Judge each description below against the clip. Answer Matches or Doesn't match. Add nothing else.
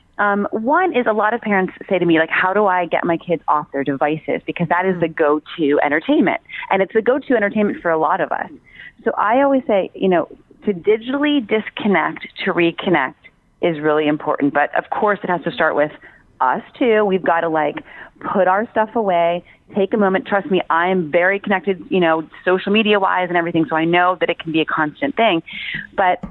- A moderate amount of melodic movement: Matches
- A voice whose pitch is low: Doesn't match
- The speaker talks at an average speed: Doesn't match